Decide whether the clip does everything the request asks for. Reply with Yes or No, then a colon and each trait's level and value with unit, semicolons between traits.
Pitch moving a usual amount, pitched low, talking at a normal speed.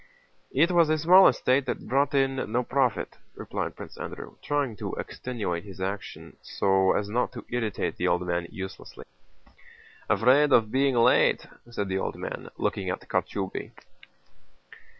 No: wide, 6.1 semitones; low, 120 Hz; average, 150 wpm